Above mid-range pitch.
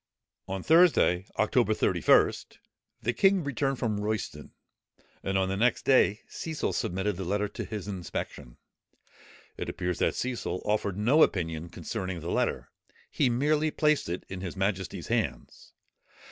No: low, 105 Hz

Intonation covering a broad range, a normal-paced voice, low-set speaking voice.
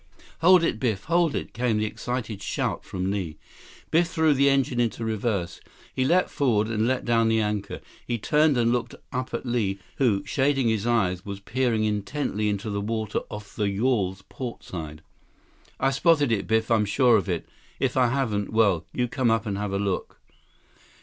No: average, 4.1 semitones; average, 185 wpm; low, 115 Hz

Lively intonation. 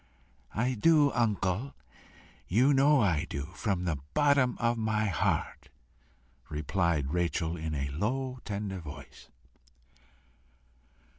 Yes: wide, 7.5 semitones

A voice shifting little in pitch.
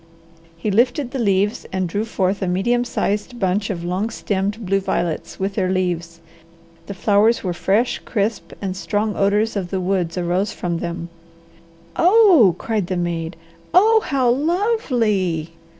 No: average, 3.9 semitones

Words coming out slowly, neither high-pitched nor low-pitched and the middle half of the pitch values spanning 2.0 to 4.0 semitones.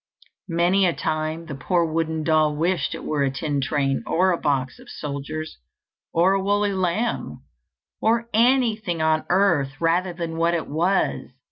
No: average, 160 wpm; medium, 165 Hz; average, 3.3 semitones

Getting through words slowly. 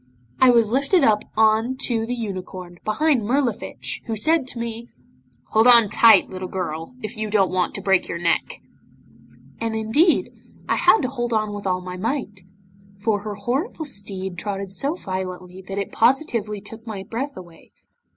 No: average, 170 wpm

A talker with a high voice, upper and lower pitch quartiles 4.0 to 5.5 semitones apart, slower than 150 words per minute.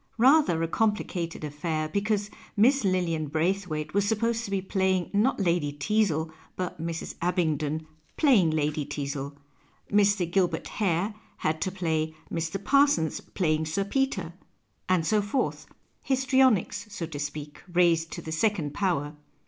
No: medium, 175 Hz; average, 4.6 semitones; average, 140 wpm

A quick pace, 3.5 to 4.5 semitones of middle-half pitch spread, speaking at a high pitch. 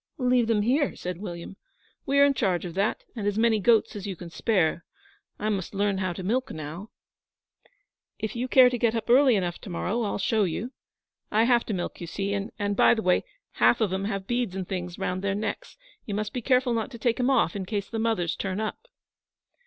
Yes: fast, 225 wpm; average, 3.8 semitones; high, 210 Hz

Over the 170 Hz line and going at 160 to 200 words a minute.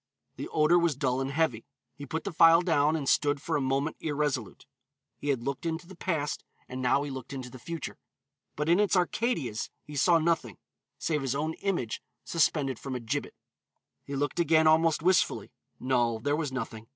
No: medium, 145 Hz; average, 190 wpm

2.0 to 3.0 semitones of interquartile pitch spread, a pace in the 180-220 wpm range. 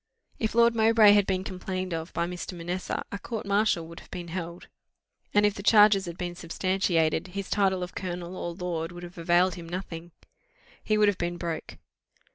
Yes: average, 2.7 semitones; average, 195 wpm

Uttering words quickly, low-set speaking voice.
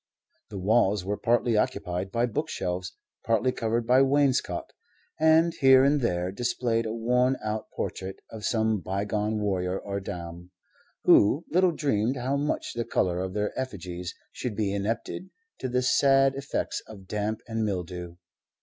No: average, 150 wpm; low, 110 Hz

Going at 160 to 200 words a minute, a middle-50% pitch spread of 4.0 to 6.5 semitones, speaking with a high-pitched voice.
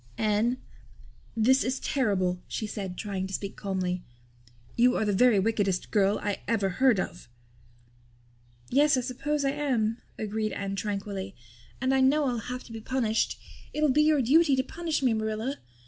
Yes: average, 165 wpm; average, 4.7 semitones; high, 225 Hz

